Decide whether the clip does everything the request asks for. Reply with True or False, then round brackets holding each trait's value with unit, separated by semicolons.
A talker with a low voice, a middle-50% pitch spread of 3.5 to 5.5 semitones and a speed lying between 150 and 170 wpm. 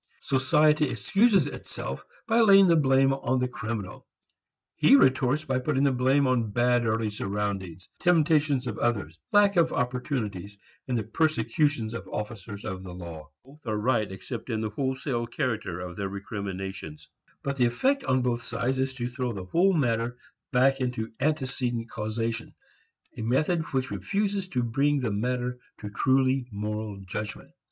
True (125 Hz; 4.2 semitones; 160 wpm)